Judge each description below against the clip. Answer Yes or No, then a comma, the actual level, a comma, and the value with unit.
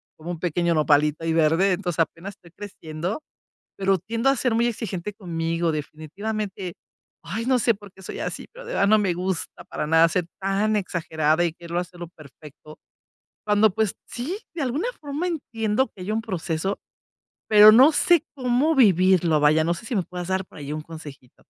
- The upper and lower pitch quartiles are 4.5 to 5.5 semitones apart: Yes, average, 5.1 semitones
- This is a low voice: No, medium, 185 Hz